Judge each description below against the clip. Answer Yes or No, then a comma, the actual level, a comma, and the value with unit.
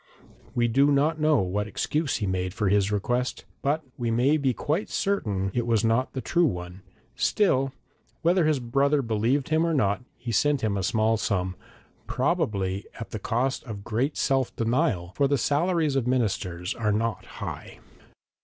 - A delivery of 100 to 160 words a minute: No, average, 170 wpm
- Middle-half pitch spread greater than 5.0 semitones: Yes, wide, 5.6 semitones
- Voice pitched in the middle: No, low, 120 Hz